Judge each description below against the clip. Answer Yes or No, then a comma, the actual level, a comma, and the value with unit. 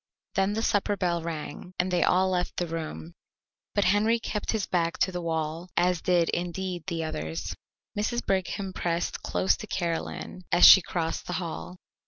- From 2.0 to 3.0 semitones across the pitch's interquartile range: Yes, narrow, 2.4 semitones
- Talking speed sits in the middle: Yes, average, 175 wpm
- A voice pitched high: No, medium, 180 Hz